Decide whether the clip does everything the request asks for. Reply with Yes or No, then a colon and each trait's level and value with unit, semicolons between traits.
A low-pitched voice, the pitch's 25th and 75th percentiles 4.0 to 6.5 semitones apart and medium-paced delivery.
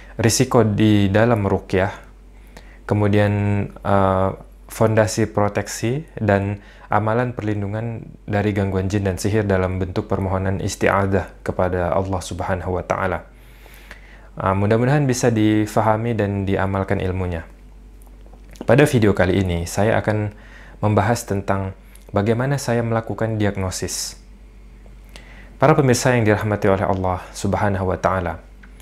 No: low, 100 Hz; narrow, 2.5 semitones; average, 110 wpm